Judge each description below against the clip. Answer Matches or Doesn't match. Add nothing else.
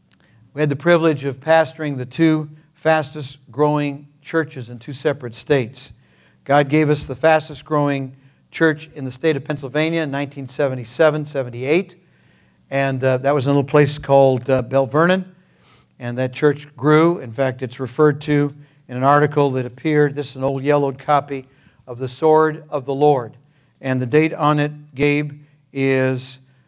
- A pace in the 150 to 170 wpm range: Matches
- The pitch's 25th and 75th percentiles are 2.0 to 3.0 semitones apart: Matches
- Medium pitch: Matches